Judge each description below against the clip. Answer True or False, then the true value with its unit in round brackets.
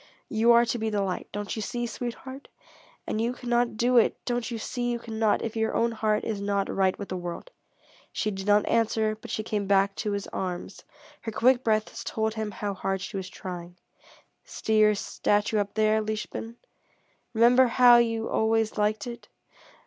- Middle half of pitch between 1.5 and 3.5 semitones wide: True (2.4 semitones)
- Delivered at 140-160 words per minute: False (190 wpm)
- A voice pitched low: False (220 Hz)